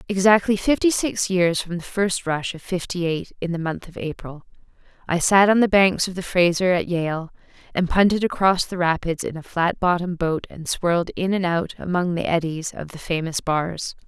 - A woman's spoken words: Yes, female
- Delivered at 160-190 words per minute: No, fast, 205 wpm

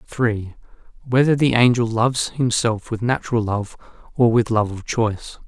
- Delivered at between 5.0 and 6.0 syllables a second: Yes, 5.3 syllables/s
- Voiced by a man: Yes, male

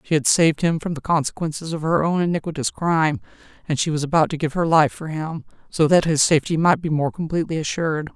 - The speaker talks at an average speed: No, fast, 230 wpm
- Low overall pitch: No, medium, 160 Hz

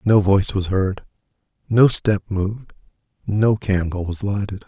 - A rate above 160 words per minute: No, average, 140 wpm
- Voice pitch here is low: Yes, low, 100 Hz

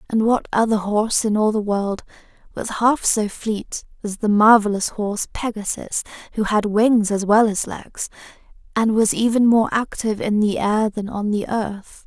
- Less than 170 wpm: No, average, 180 wpm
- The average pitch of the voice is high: Yes, high, 215 Hz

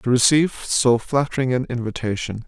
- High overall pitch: No, low, 125 Hz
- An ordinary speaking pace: Yes, average, 145 wpm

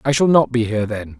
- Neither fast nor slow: No, fast, 300 wpm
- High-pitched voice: No, low, 120 Hz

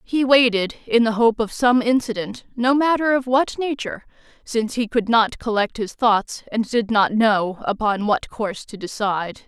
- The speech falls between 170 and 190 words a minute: Yes, average, 185 wpm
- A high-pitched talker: Yes, high, 225 Hz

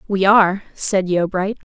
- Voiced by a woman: Yes, female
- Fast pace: No, average, 140 wpm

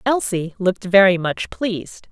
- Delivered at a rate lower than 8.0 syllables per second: Yes, 4.7 syllables/s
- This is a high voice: Yes, high, 195 Hz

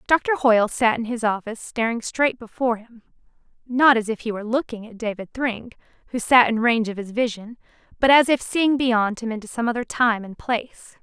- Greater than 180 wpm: Yes, fast, 205 wpm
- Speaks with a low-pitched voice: No, high, 235 Hz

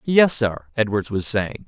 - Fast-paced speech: No, average, 180 wpm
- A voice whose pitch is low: Yes, low, 115 Hz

